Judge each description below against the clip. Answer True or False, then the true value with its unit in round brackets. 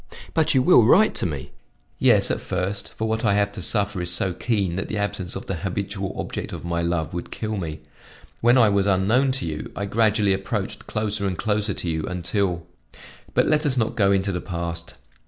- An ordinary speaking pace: False (210 wpm)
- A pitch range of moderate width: True (3.6 semitones)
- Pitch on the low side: True (100 Hz)